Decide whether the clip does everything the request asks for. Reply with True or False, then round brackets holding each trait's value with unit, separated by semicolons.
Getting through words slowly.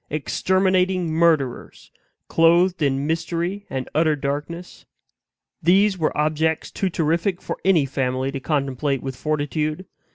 True (120 wpm)